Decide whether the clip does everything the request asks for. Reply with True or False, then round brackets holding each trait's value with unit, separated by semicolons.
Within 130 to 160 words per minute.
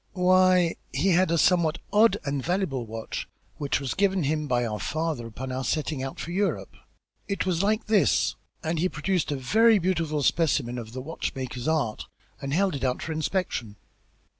False (180 wpm)